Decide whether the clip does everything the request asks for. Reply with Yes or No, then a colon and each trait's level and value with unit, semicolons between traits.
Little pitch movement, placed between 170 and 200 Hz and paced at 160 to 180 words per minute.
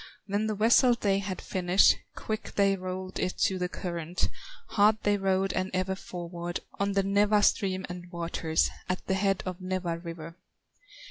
Yes: narrow, 2.0 semitones; medium, 185 Hz; average, 165 wpm